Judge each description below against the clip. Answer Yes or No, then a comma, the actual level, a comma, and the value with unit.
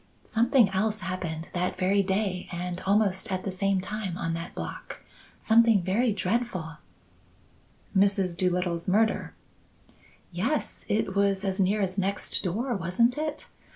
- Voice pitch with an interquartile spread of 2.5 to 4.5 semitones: Yes, average, 2.9 semitones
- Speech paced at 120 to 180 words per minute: Yes, average, 140 wpm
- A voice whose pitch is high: Yes, high, 195 Hz